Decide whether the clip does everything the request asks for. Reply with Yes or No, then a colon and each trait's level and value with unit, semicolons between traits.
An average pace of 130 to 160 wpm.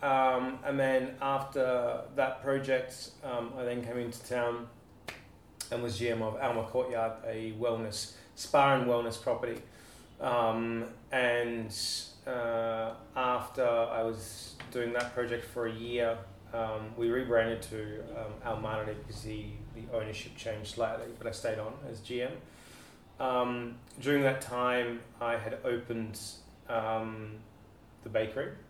Yes: slow, 135 wpm